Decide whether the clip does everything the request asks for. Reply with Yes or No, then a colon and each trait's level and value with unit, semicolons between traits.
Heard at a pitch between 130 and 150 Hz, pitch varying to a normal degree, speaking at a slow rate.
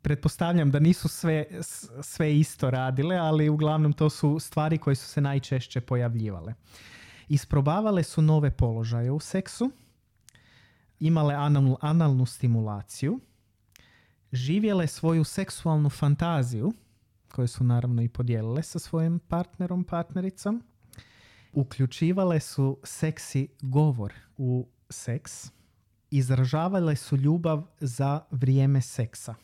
Yes: medium, 140 Hz; average, 4.5 semitones; slow, 105 wpm